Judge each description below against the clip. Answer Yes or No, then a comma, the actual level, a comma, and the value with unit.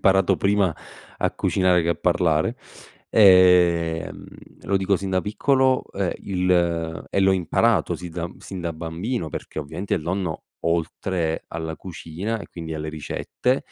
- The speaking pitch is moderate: No, very low, 90 Hz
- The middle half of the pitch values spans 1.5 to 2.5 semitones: No, average, 2.9 semitones